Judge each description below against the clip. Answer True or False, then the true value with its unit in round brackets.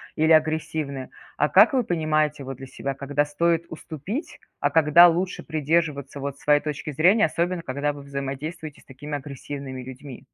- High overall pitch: False (150 Hz)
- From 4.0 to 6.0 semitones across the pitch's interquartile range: False (2.7 semitones)